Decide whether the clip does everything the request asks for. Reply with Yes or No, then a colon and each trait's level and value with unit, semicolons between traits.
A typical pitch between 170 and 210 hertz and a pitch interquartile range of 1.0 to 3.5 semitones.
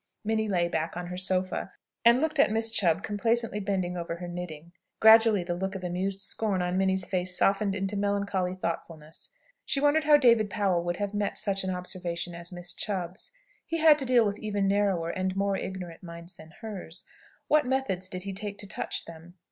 Yes: high, 190 Hz; average, 3.0 semitones